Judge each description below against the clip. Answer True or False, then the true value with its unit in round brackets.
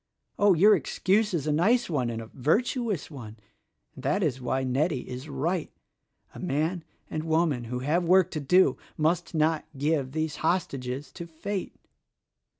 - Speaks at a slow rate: False (160 wpm)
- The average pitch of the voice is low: False (155 Hz)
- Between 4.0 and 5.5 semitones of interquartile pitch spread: True (5.0 semitones)